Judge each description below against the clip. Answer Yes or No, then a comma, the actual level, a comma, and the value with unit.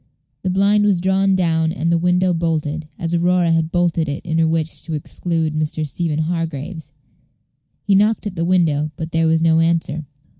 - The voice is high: No, medium, 165 Hz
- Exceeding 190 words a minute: No, average, 185 wpm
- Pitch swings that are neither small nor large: No, narrow, 2.0 semitones